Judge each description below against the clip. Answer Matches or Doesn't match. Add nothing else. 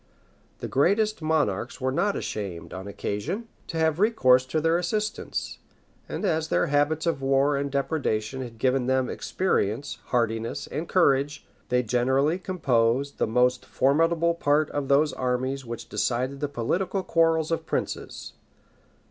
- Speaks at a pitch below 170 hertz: Matches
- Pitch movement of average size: Matches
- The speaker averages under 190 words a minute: Matches